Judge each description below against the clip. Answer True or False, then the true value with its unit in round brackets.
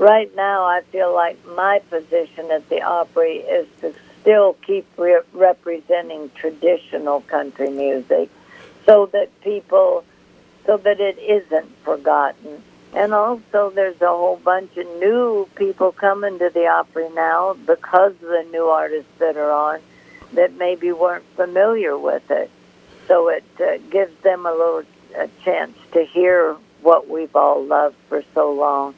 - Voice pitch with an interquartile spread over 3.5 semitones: True (3.9 semitones)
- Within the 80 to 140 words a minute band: False (150 wpm)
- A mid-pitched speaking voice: True (180 Hz)